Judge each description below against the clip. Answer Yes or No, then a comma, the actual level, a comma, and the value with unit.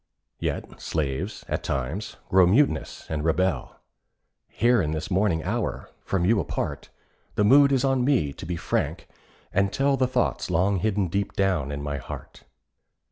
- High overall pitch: No, very low, 95 Hz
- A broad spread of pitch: Yes, wide, 5.8 semitones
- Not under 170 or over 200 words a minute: No, average, 160 wpm